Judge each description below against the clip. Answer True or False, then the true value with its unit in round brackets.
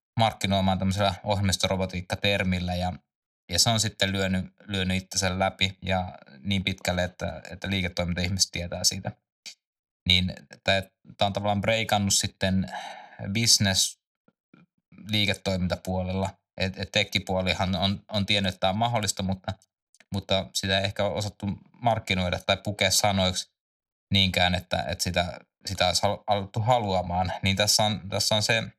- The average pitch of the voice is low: True (95 Hz)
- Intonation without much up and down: True (1.6 semitones)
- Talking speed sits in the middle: True (130 wpm)